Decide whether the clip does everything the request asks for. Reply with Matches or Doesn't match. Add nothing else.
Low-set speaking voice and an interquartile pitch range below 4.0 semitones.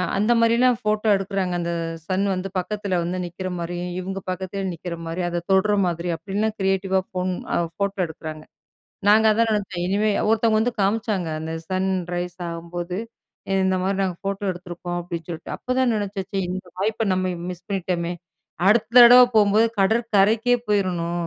Doesn't match